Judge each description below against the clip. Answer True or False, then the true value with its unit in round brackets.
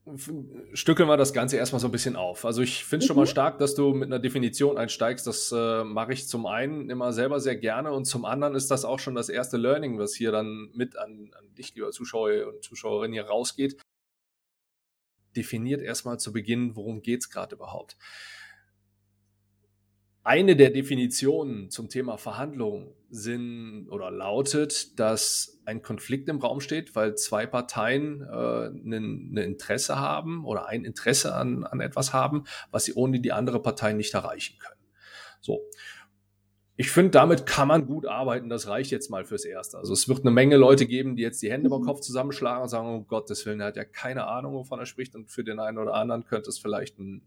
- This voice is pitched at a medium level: False (125 Hz)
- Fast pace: True (195 wpm)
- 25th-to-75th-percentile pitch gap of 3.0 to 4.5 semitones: True (4.0 semitones)